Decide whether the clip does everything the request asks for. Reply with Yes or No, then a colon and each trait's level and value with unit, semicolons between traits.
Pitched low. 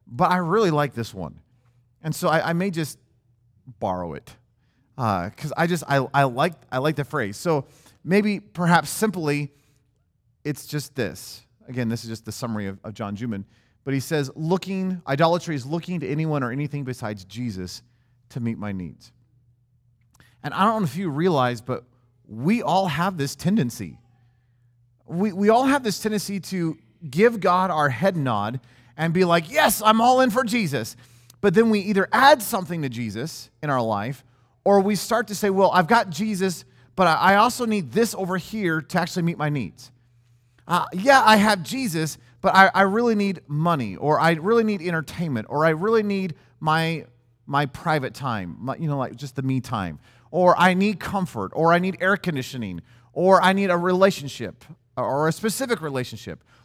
No: medium, 150 Hz